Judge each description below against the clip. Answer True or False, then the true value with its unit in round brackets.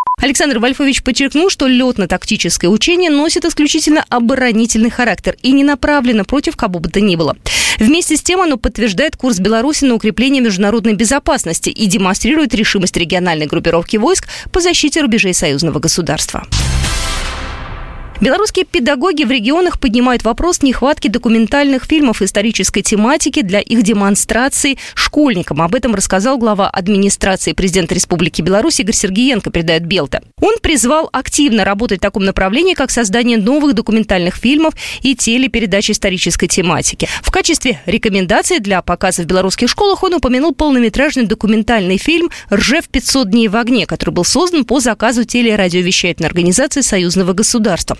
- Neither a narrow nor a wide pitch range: False (6.5 semitones)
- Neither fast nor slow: True (140 wpm)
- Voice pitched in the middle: False (230 Hz)